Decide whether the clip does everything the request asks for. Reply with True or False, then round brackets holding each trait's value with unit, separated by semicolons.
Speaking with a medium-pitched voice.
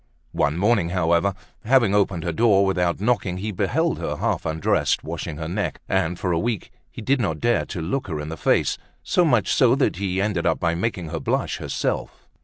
False (95 Hz)